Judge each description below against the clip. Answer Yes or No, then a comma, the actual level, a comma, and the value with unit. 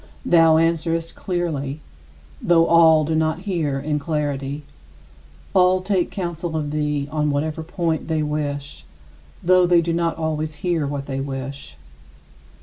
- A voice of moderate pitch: Yes, medium, 160 Hz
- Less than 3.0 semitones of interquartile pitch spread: Yes, narrow, 2.4 semitones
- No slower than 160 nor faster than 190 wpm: No, average, 140 wpm